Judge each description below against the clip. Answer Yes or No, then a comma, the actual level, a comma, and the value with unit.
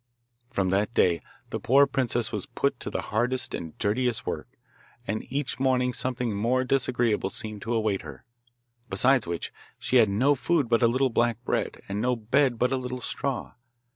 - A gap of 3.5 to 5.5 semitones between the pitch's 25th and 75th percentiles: No, average, 3.1 semitones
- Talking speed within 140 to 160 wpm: No, average, 180 wpm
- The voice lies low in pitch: Yes, low, 120 Hz